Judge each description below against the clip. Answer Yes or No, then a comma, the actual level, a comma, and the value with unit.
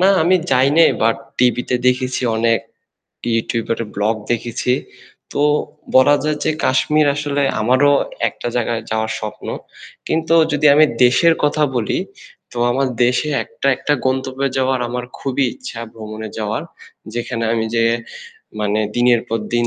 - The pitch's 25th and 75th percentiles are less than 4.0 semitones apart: Yes, average, 3.6 semitones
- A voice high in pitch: No, low, 125 Hz